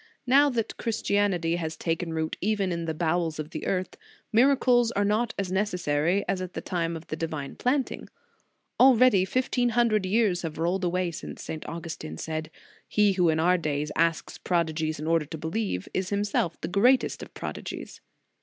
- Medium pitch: Yes, medium, 180 Hz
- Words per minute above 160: Yes, average, 180 wpm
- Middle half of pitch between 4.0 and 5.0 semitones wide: Yes, average, 4.5 semitones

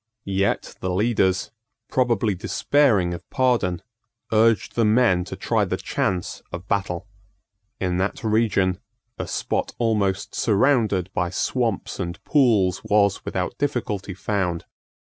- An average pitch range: Yes, average, 3.8 semitones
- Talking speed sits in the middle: No, slow, 125 wpm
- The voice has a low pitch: Yes, low, 100 Hz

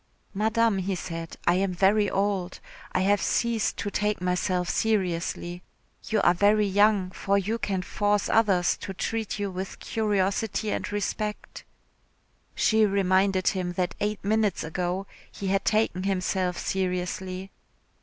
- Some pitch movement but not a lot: No, narrow, 2.3 semitones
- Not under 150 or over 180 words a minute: No, average, 140 wpm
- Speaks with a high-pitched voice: Yes, high, 195 Hz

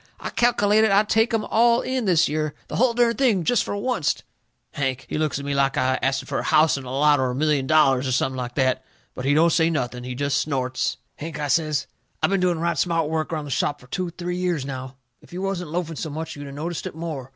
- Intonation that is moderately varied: Yes, average, 4.9 semitones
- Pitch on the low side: No, medium, 155 Hz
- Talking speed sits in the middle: No, fast, 250 wpm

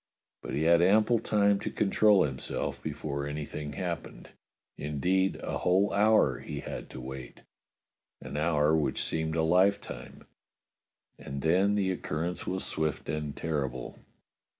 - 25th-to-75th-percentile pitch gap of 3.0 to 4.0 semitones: No, average, 4.5 semitones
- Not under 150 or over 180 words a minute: No, average, 140 wpm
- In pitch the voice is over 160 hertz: No, very low, 80 Hz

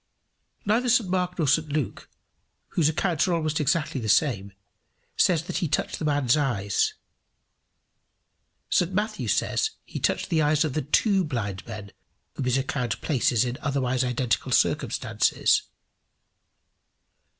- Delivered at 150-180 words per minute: No, average, 140 wpm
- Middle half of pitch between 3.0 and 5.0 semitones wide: No, wide, 5.5 semitones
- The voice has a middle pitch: Yes, medium, 150 Hz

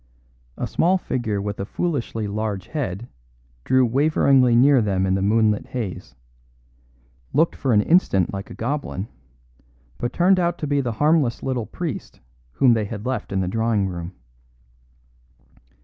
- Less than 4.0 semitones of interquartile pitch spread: No, wide, 5.5 semitones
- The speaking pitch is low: Yes, low, 115 Hz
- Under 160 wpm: Yes, average, 150 wpm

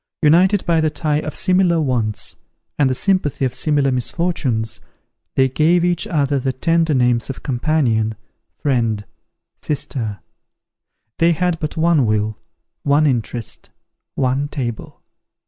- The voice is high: No, medium, 140 Hz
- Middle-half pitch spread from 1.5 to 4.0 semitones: No, average, 5.1 semitones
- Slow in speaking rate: Yes, slow, 130 wpm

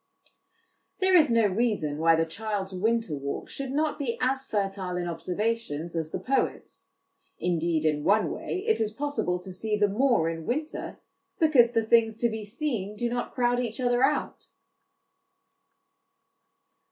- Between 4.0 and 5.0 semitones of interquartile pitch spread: No, wide, 5.5 semitones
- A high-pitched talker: Yes, high, 220 Hz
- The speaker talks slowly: No, average, 155 wpm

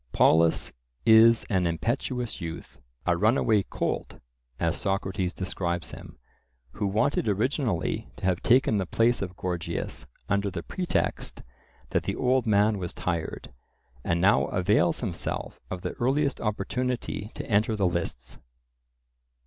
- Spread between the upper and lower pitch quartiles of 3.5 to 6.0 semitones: Yes, average, 4.6 semitones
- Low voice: Yes, low, 100 Hz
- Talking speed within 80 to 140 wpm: Yes, slow, 135 wpm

